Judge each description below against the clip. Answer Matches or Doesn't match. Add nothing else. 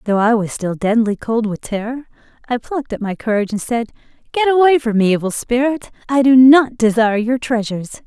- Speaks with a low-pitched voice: Doesn't match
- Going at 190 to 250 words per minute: Matches